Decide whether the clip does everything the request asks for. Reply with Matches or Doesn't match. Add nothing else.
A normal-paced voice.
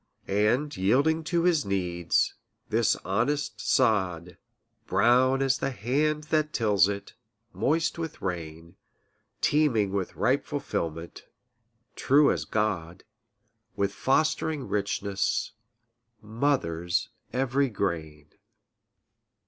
Doesn't match